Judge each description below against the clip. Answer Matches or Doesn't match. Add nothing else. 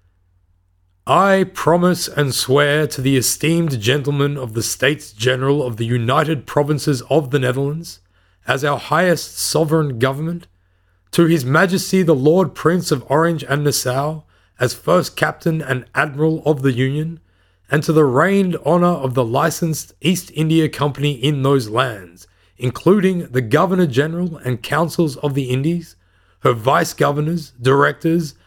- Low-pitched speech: Doesn't match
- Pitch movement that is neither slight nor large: Matches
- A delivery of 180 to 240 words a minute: Doesn't match